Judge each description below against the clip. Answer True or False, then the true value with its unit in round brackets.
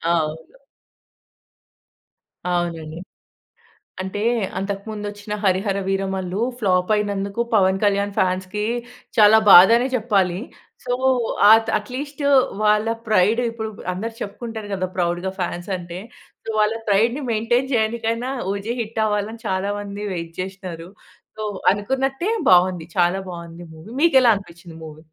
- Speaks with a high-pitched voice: True (200 Hz)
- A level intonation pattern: False (3.3 semitones)